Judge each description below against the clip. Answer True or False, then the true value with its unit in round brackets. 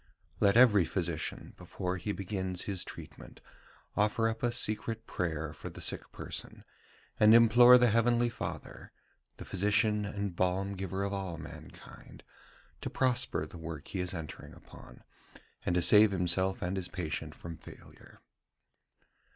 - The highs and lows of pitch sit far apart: False (3.5 semitones)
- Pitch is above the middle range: False (95 Hz)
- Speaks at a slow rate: False (145 wpm)